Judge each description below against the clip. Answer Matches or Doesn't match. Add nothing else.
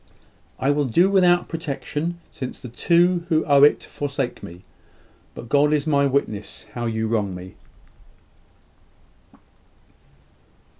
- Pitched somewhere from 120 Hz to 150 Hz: Matches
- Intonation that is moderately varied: Doesn't match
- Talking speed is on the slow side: Matches